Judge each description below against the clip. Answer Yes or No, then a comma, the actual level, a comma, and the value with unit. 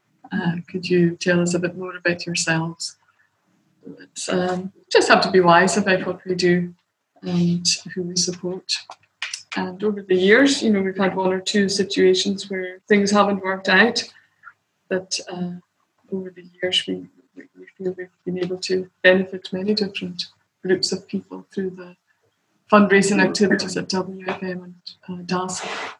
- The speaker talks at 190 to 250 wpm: No, average, 155 wpm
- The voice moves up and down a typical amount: No, narrow, 1.4 semitones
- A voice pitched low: No, medium, 185 Hz